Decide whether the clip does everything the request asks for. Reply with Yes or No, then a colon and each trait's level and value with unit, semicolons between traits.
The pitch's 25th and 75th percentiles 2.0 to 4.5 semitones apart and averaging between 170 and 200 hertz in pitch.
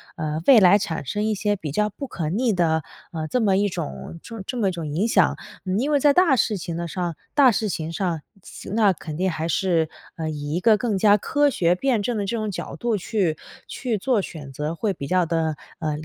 No: average, 5.1 semitones; high, 190 Hz